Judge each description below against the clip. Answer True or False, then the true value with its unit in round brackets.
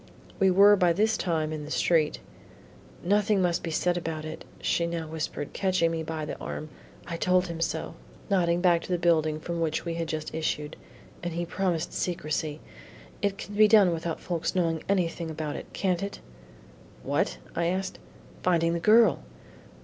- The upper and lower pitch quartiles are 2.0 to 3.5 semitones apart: True (2.4 semitones)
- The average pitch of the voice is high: False (170 Hz)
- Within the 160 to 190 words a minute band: True (180 wpm)